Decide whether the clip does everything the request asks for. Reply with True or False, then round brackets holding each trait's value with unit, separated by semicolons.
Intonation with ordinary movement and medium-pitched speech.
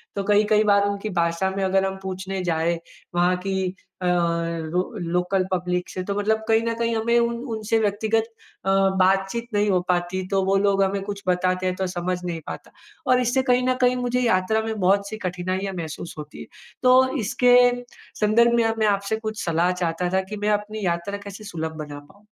False (3.2 semitones; 195 Hz)